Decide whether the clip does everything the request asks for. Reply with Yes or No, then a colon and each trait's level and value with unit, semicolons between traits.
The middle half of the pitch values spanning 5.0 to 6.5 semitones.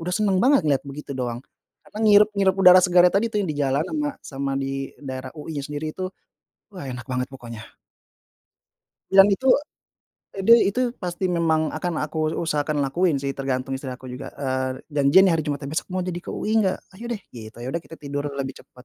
Yes: wide, 5.6 semitones